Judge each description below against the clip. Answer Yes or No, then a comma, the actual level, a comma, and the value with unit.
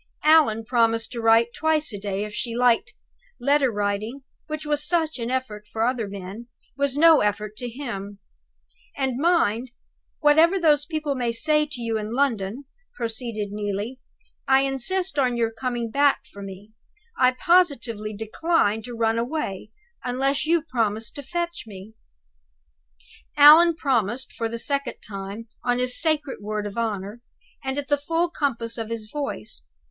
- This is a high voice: Yes, high, 245 Hz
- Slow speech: No, average, 155 wpm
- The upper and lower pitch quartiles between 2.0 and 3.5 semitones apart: No, average, 4.9 semitones